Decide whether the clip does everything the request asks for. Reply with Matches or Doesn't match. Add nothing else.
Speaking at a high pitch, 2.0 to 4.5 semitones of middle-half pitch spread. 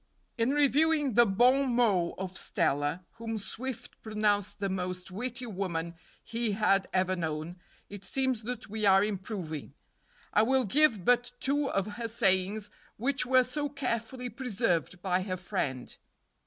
Doesn't match